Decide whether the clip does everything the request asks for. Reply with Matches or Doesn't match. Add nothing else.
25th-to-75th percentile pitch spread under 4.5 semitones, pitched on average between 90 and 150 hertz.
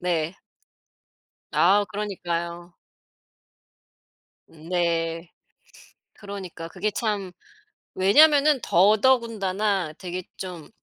Doesn't match